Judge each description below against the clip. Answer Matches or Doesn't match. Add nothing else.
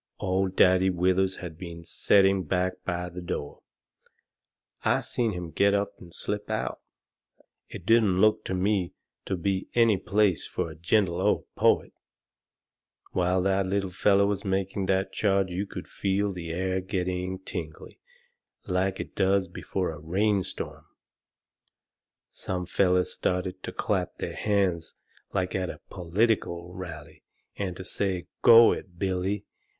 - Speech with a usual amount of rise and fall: Doesn't match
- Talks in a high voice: Doesn't match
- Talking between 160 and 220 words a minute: Doesn't match